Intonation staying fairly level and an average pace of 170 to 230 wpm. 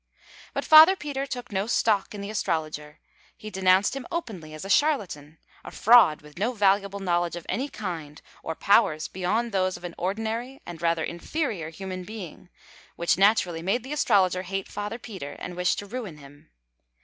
No: average, 4.7 semitones; average, 175 wpm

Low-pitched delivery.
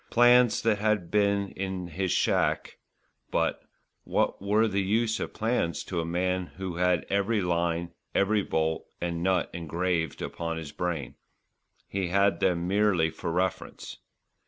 Yes: very low, 95 Hz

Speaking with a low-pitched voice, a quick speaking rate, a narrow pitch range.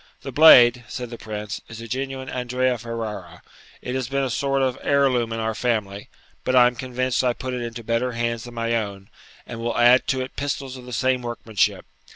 Yes: low, 120 Hz; fast, 215 wpm; narrow, 1.9 semitones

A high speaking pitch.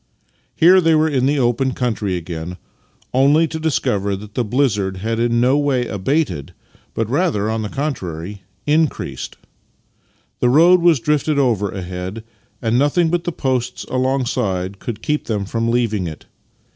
No: low, 120 Hz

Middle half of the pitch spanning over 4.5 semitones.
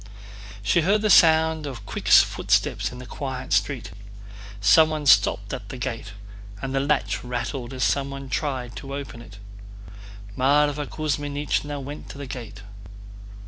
No: average, 3.1 semitones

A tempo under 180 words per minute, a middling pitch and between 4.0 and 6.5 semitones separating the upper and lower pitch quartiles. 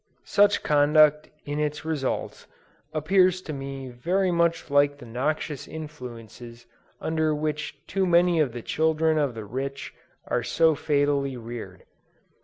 No: slow, 135 wpm; medium, 150 Hz; average, 3.1 semitones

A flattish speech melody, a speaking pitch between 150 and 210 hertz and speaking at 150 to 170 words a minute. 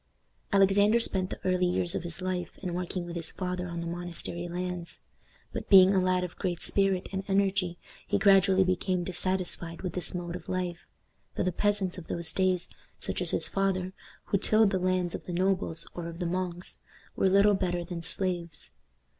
No: narrow, 1.6 semitones; medium, 185 Hz; average, 190 wpm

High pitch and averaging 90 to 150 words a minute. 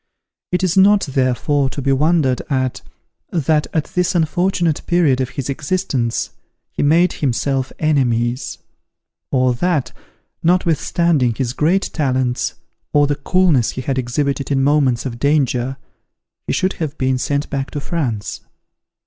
No: medium, 140 Hz; average, 140 wpm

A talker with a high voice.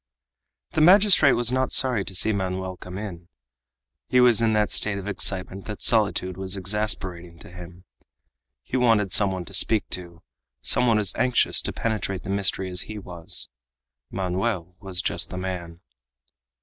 No: very low, 95 Hz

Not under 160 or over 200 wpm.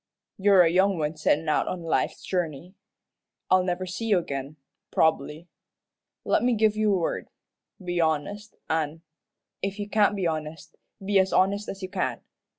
Yes: average, 165 wpm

